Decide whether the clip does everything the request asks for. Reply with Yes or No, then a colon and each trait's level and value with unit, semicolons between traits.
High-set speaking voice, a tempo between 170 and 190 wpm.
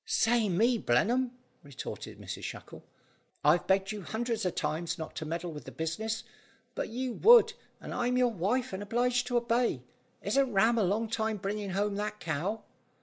Yes: high, 220 Hz; average, 175 wpm